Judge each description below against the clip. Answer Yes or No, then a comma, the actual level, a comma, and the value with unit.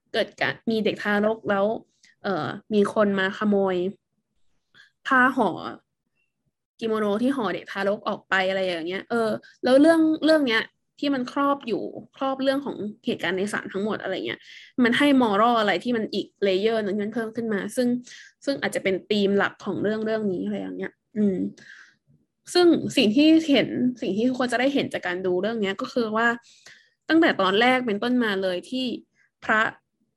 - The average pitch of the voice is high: Yes, high, 225 Hz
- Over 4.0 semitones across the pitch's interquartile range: Yes, average, 4.5 semitones